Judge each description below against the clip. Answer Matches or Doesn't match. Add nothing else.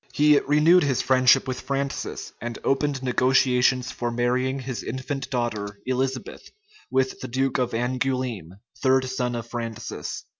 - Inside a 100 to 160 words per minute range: Matches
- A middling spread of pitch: Doesn't match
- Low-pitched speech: Matches